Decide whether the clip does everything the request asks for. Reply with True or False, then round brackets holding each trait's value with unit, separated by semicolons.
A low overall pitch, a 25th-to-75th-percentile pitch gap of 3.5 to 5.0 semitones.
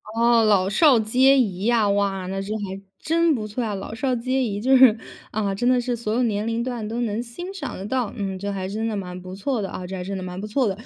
False (215 Hz; 3.9 semitones)